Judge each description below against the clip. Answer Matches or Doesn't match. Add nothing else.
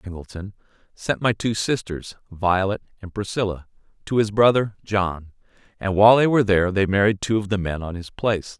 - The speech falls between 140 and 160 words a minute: Doesn't match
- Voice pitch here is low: Matches